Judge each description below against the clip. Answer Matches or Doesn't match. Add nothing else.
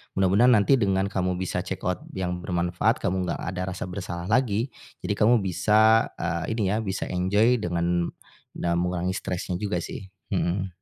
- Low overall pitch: Matches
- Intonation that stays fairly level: Doesn't match